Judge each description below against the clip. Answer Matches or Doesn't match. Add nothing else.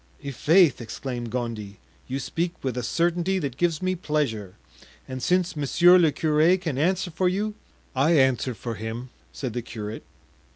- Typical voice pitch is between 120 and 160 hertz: Matches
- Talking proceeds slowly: Doesn't match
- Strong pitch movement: Matches